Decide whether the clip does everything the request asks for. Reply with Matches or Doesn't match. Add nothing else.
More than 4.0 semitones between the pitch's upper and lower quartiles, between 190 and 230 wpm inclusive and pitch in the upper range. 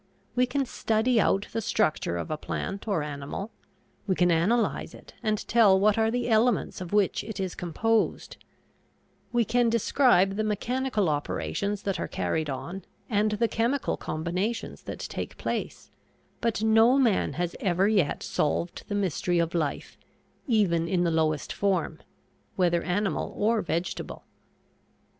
Doesn't match